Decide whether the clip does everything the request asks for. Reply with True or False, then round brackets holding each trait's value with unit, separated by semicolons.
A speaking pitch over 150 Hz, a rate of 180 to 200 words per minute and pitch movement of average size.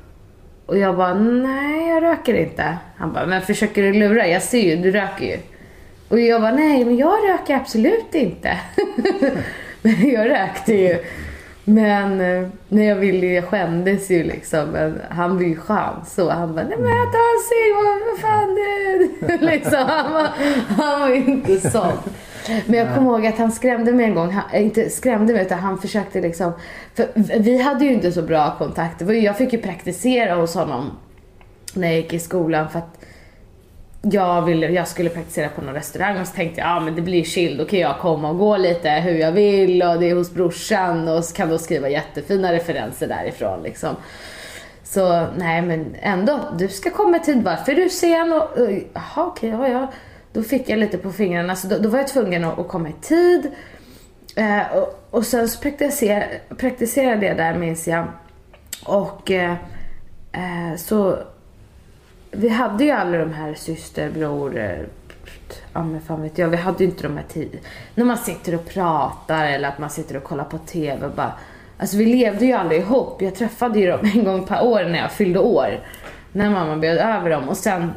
False (190 Hz; 190 wpm; 6.2 semitones)